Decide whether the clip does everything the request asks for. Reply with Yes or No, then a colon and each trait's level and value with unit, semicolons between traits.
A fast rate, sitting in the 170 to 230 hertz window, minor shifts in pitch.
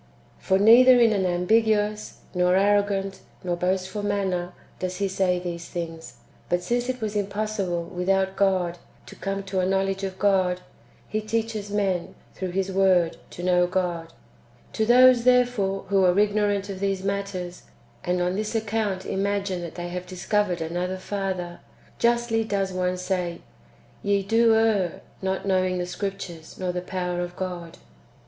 No: average, 160 wpm; high, 190 Hz; narrow, 2.3 semitones